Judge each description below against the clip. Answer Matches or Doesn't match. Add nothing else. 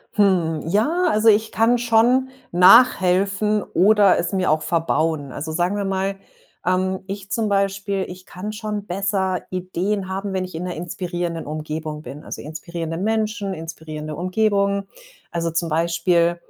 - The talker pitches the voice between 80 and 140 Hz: Doesn't match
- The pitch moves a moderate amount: Matches